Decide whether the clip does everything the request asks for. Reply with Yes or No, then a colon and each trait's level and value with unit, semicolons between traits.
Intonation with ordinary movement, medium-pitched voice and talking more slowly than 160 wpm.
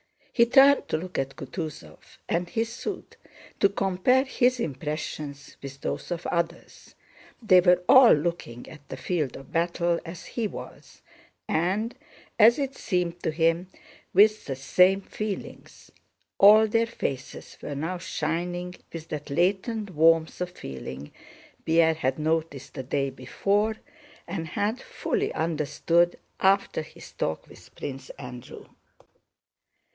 Yes: average, 4.9 semitones; medium, 170 Hz; slow, 135 wpm